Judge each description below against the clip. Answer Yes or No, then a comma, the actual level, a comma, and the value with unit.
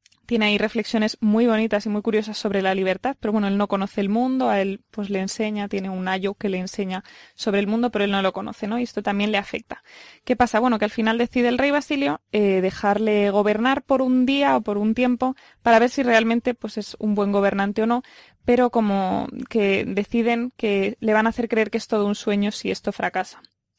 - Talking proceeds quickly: Yes, fast, 230 wpm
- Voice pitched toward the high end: Yes, high, 215 Hz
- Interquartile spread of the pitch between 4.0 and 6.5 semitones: No, average, 2.8 semitones